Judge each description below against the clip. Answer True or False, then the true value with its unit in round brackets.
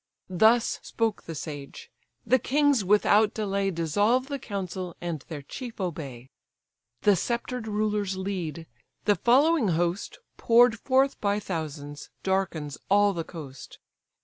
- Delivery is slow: True (125 wpm)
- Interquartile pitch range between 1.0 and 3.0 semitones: False (5.5 semitones)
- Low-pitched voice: False (200 Hz)